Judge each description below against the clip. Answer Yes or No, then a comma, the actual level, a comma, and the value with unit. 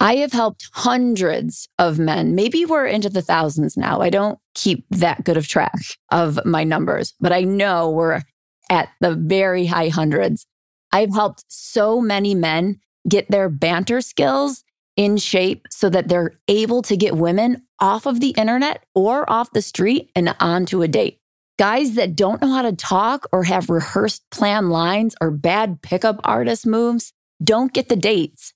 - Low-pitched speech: No, high, 195 Hz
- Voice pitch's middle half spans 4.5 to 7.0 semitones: Yes, average, 4.8 semitones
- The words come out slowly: No, average, 170 wpm